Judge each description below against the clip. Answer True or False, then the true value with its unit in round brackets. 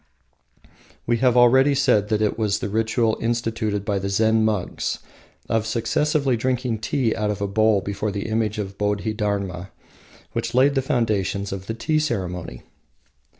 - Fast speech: False (160 wpm)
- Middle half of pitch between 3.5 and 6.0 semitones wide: False (2.8 semitones)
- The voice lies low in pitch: True (110 Hz)